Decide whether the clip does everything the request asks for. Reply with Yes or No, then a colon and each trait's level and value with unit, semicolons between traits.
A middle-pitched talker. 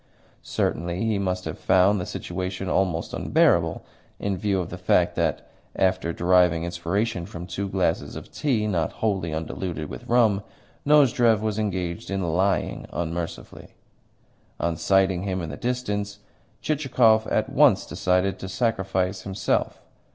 No: very low, 95 Hz